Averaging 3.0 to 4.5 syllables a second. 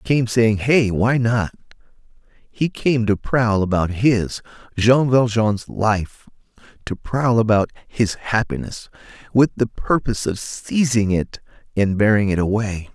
Yes: 3.9 syllables/s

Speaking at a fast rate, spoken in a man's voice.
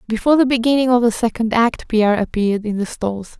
No: fast, 210 wpm; female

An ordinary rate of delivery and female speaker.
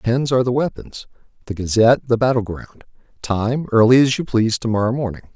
No: average, 180 wpm; male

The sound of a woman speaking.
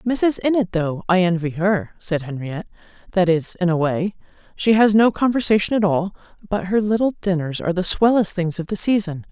Yes: female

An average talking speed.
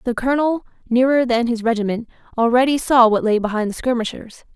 Yes: average, 170 wpm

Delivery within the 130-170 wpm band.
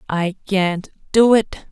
Yes: average, 140 wpm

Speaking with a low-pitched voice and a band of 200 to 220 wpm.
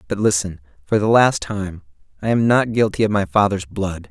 Yes: low, 100 Hz; fast, 205 wpm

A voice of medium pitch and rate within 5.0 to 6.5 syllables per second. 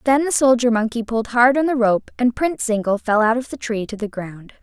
No: high, 235 Hz; 5.7 syllables/s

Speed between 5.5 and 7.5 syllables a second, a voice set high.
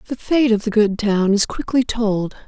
No: 4.6 syllables/s; high, 220 Hz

